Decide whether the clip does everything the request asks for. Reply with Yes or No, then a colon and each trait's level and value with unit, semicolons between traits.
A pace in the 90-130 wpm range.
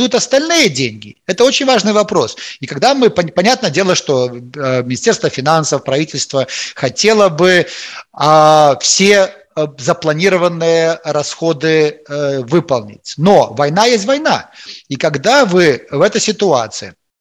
Yes: average, 110 wpm